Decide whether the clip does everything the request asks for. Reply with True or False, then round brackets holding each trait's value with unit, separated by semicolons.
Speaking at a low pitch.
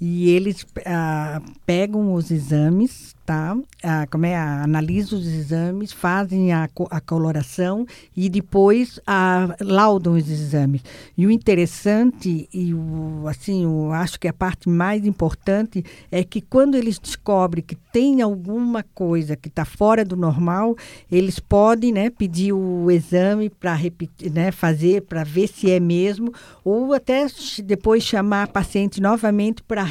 False (185 Hz)